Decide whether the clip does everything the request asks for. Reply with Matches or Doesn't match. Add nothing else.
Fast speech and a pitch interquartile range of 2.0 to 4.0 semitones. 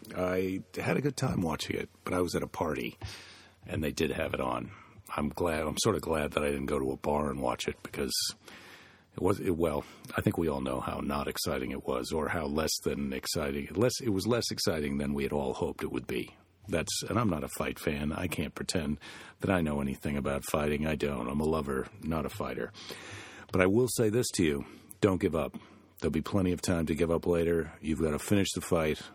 Doesn't match